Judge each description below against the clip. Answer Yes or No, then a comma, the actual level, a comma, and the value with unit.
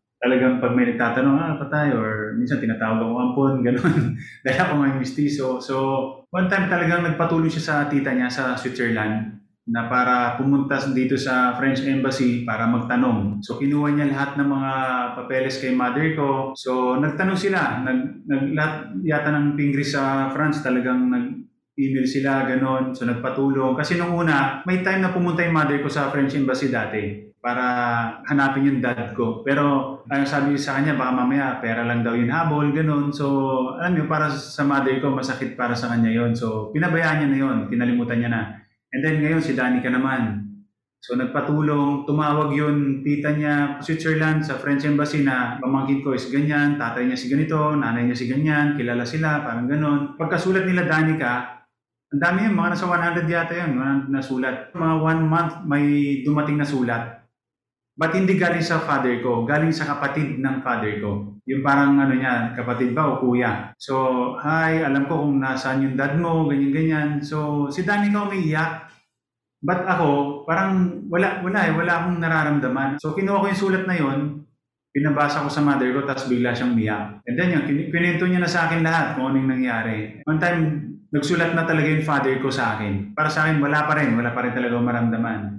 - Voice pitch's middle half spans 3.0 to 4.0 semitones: Yes, average, 3.5 semitones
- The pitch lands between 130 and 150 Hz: Yes, medium, 140 Hz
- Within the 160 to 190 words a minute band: Yes, average, 185 wpm